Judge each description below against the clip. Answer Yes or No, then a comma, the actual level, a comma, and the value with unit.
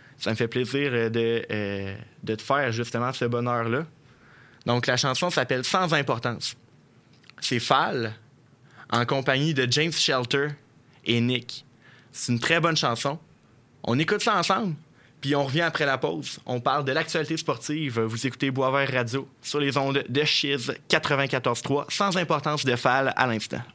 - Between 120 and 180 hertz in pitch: Yes, low, 135 Hz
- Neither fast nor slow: Yes, average, 155 wpm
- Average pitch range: Yes, average, 3.6 semitones